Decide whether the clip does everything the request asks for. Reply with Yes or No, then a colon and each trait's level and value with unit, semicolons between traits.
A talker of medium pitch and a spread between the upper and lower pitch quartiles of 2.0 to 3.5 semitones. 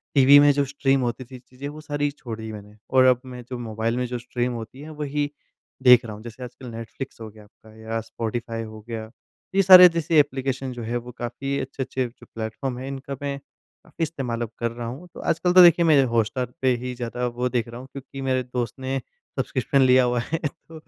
No: low, 125 Hz; average, 2.9 semitones